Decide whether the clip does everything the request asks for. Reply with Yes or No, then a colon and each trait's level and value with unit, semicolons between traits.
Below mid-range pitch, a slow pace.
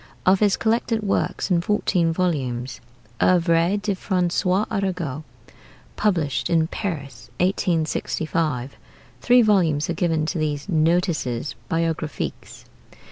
No: medium, 170 Hz; slow, 105 wpm